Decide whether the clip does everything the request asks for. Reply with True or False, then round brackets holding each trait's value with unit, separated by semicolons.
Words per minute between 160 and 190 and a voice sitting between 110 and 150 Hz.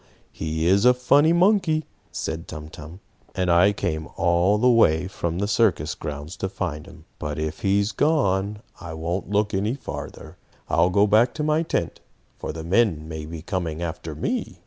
False (185 wpm; 95 Hz)